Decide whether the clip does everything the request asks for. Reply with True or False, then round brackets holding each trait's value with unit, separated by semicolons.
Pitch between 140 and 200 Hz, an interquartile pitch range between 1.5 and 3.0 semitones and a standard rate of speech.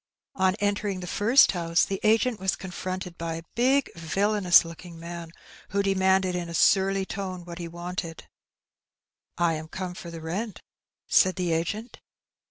True (185 Hz; 2.6 semitones; 160 wpm)